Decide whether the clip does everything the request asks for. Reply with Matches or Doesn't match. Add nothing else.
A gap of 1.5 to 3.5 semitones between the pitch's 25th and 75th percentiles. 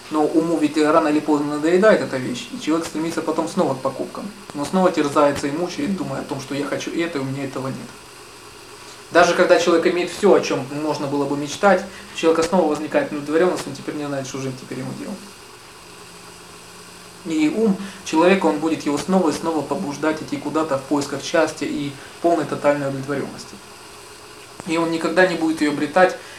Matches